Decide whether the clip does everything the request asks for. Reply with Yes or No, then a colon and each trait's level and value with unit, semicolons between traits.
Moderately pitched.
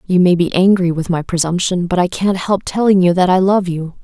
Yes: medium, 180 Hz